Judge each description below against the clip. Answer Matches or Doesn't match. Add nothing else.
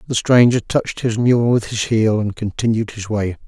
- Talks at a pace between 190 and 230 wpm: Matches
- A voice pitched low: Matches